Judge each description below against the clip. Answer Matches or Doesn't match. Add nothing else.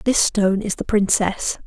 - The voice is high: Matches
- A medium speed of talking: Matches